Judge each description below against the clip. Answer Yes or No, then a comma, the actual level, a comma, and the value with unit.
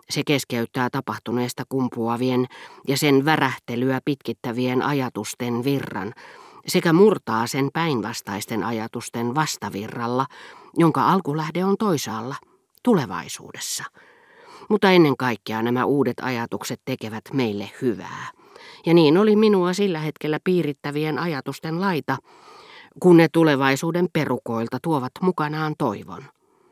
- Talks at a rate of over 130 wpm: No, average, 105 wpm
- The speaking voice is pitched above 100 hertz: Yes, low, 135 Hz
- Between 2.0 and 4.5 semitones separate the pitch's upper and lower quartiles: No, average, 5.2 semitones